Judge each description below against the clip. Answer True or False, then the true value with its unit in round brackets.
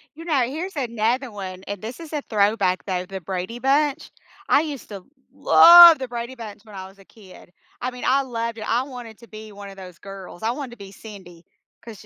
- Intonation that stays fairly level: False (4.9 semitones)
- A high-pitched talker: True (225 Hz)